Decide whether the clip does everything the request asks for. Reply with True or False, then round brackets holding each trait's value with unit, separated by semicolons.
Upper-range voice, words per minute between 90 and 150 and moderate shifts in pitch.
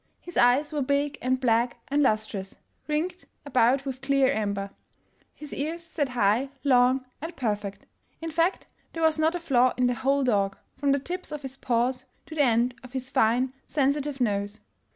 False (265 Hz; 180 wpm; 3.3 semitones)